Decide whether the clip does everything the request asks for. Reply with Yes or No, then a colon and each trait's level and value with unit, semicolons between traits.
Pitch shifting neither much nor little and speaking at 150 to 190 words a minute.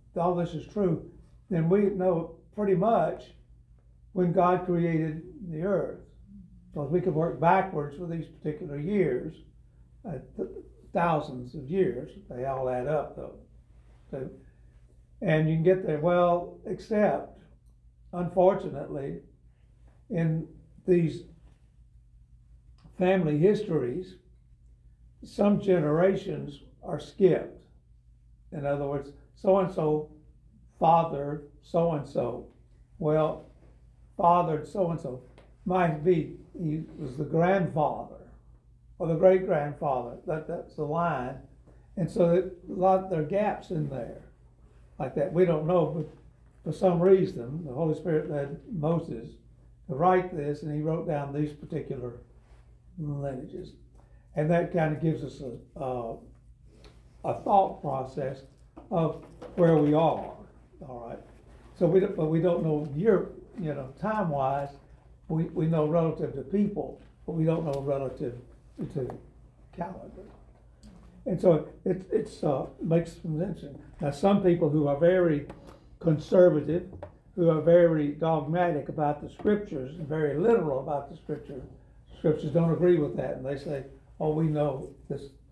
No: average, 3.6 semitones; average, 140 wpm